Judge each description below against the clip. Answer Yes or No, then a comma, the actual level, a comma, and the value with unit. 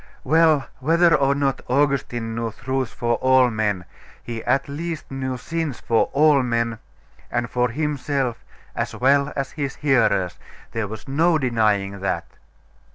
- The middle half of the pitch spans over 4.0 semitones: No, average, 3.6 semitones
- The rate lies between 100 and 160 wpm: Yes, average, 145 wpm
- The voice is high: No, low, 130 Hz